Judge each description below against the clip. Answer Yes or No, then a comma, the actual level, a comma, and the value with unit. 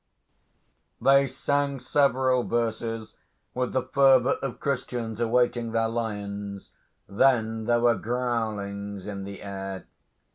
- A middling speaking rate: No, slow, 110 wpm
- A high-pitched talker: No, low, 115 Hz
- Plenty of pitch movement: No, average, 3.7 semitones